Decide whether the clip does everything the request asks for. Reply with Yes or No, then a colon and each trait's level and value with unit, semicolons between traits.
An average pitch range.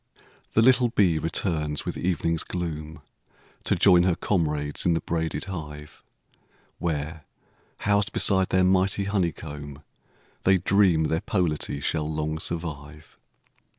Yes: average, 3.5 semitones